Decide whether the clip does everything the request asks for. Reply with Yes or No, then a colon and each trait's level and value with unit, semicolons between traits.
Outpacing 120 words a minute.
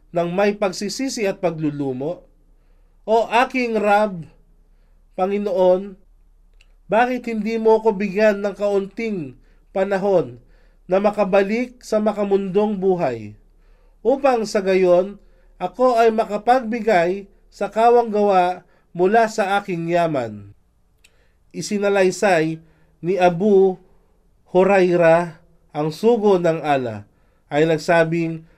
No: slow, 95 wpm